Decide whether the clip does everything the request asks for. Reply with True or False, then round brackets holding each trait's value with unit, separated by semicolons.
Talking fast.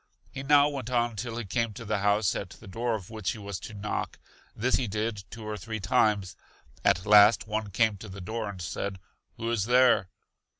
True (215 wpm)